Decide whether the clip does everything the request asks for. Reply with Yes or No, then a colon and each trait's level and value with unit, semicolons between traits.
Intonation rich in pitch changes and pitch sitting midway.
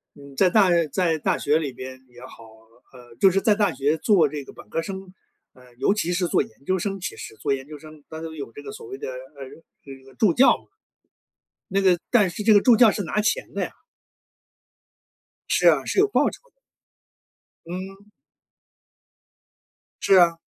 Yes: wide, 6.2 semitones; medium, 175 Hz